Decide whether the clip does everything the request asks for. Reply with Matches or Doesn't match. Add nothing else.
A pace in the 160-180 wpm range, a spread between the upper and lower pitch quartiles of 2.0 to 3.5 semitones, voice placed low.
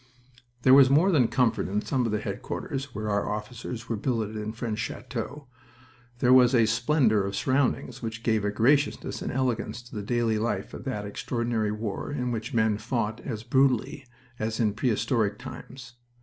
Matches